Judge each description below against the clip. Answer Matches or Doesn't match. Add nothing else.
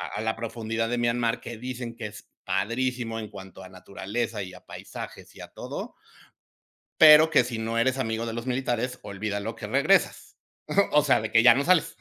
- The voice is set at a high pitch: Doesn't match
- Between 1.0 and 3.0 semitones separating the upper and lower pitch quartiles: Matches